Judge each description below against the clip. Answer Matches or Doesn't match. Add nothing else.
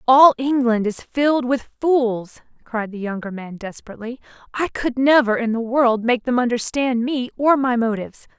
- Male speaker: Doesn't match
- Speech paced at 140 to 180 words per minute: Matches